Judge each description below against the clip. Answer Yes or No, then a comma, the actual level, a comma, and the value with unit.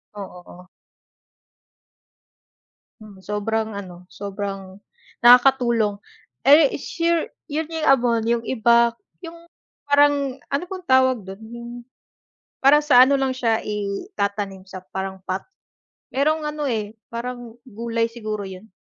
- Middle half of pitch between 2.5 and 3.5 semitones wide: No, average, 5.1 semitones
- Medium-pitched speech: No, high, 235 Hz